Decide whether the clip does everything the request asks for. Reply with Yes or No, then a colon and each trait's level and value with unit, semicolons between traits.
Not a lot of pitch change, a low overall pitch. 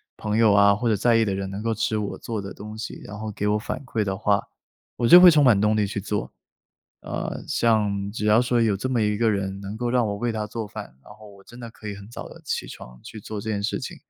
Yes: narrow, 2.2 semitones; low, 105 Hz